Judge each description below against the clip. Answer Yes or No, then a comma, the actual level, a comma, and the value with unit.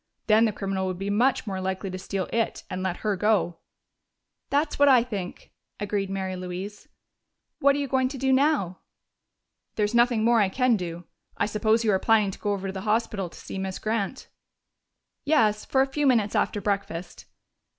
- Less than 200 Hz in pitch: No, high, 210 Hz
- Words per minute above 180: Yes, average, 190 wpm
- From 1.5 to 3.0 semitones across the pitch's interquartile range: No, average, 3.9 semitones